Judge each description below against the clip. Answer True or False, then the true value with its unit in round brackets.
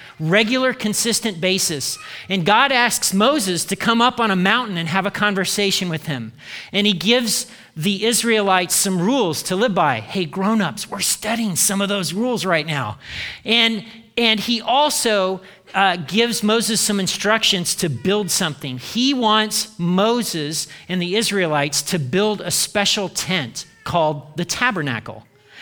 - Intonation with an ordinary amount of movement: True (4.1 semitones)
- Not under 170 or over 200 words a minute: False (150 wpm)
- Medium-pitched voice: False (195 Hz)